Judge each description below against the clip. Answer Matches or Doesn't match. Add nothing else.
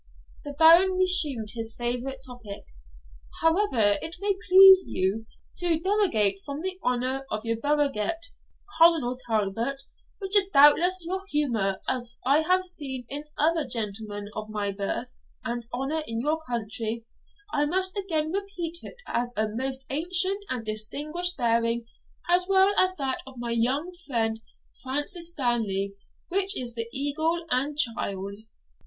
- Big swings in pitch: Matches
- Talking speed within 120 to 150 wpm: Matches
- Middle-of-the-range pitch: Doesn't match